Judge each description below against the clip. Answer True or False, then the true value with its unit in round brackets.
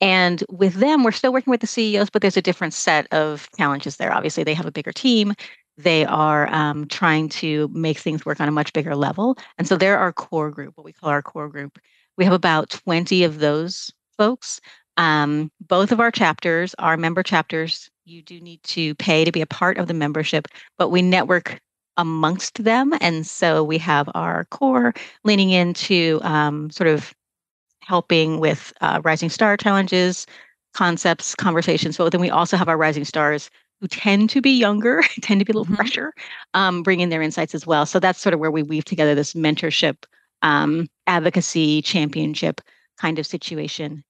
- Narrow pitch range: False (3.7 semitones)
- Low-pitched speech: False (170 Hz)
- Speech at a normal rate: True (190 wpm)